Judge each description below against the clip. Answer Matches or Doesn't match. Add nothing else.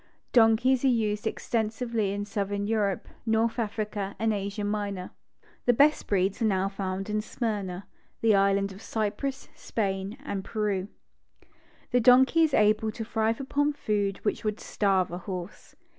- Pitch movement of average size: Doesn't match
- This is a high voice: Matches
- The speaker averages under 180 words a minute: Matches